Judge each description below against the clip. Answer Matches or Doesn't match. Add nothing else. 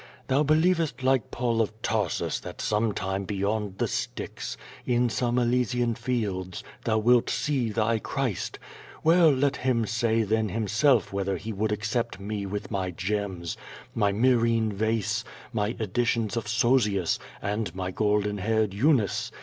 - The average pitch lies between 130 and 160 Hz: Doesn't match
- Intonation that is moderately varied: Matches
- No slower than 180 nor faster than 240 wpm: Doesn't match